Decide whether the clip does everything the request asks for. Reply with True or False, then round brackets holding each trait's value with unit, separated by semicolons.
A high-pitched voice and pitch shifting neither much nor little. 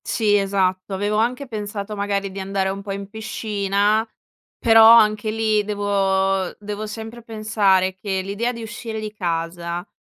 False (205 Hz; 2.0 semitones)